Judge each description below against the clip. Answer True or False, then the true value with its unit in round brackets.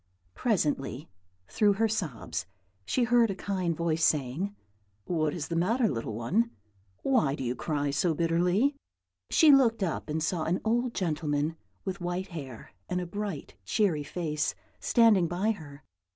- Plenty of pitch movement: True (5.7 semitones)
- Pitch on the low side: False (175 Hz)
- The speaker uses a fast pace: False (150 wpm)